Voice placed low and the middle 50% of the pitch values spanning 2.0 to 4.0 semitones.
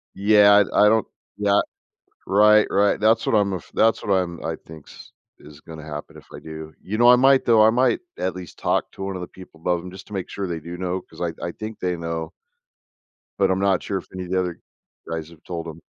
Yes: very low, 95 Hz; average, 3.6 semitones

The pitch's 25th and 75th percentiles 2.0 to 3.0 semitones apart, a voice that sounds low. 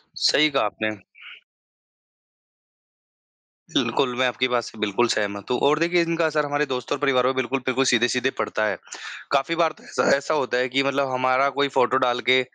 Yes: narrow, 2.5 semitones; low, 130 Hz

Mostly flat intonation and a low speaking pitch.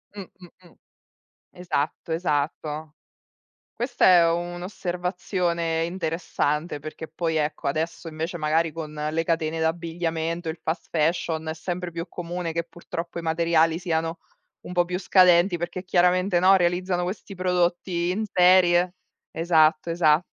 No: narrow, 1.8 semitones; medium, 170 Hz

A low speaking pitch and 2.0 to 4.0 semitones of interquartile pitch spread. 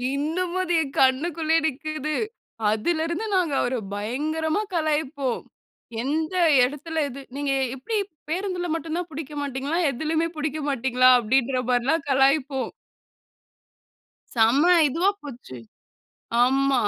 No: very high, 295 Hz; average, 3.5 semitones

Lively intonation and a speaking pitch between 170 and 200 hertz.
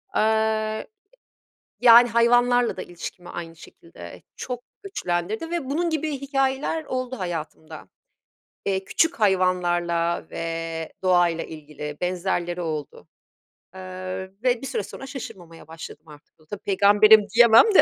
Yes: wide, 6.6 semitones; high, 190 Hz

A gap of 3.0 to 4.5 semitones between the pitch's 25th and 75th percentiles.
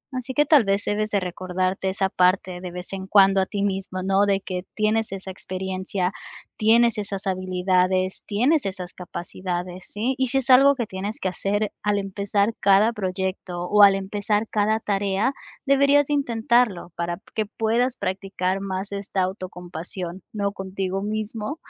No: narrow, 2.5 semitones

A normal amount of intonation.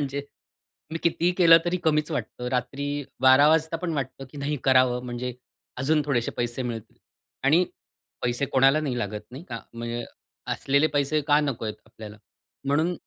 Yes: average, 3.7 semitones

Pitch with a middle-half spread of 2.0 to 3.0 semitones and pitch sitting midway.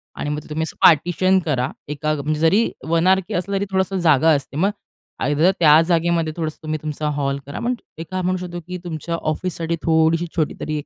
Yes: average, 2.7 semitones; medium, 160 Hz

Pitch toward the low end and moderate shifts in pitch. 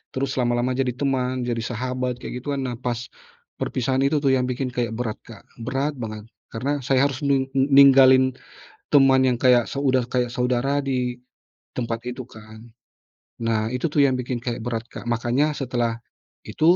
No: low, 125 Hz; narrow, 1.8 semitones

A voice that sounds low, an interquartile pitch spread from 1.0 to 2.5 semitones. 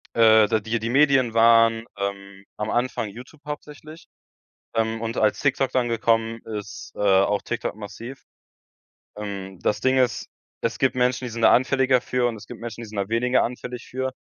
No: low, 115 Hz; average, 2.9 semitones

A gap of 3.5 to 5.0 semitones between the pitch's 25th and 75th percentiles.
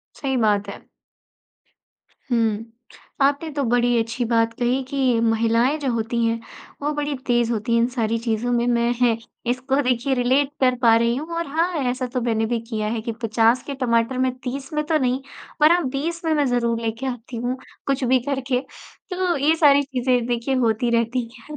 No: average, 2.9 semitones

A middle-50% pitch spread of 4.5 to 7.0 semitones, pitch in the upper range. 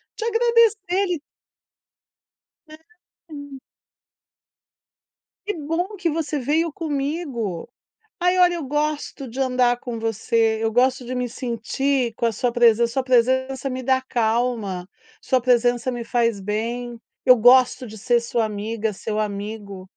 No: average, 4.1 semitones; very high, 250 Hz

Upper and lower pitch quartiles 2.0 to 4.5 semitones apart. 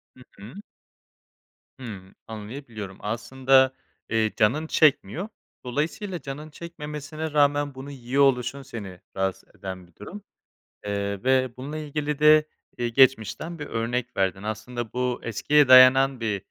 No: average, 5.1 semitones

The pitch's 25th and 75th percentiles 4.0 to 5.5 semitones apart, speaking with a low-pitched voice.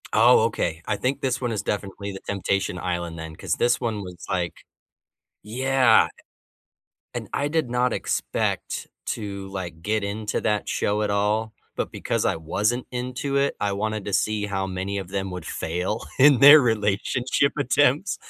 Yes: average, 4.3 semitones; low, 105 Hz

